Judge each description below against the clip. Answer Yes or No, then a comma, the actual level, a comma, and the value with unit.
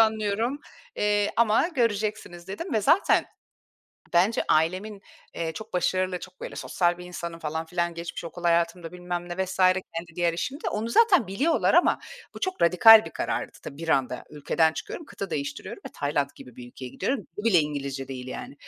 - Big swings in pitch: No, average, 4.5 semitones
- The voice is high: No, medium, 180 Hz